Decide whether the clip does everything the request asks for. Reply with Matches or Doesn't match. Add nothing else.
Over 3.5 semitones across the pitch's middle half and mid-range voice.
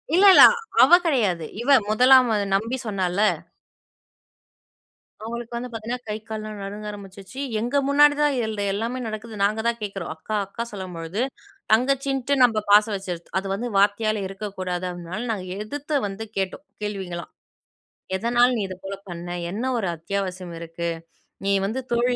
Doesn't match